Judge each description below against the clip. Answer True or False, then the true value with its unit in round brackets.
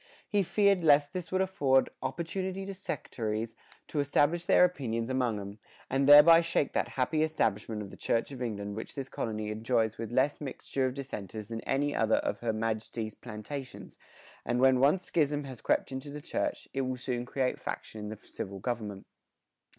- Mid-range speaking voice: False (130 Hz)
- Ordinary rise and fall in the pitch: True (4.8 semitones)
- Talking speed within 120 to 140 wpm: False (180 wpm)